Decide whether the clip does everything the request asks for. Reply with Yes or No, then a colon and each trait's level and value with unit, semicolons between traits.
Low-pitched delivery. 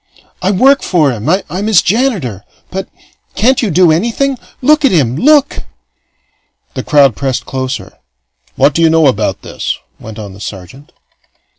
No: medium, 165 Hz